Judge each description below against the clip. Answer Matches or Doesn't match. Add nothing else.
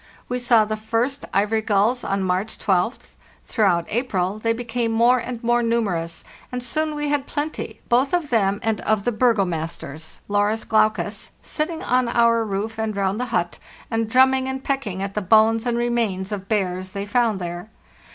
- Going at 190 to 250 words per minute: Doesn't match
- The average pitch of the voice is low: Doesn't match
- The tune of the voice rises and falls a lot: Doesn't match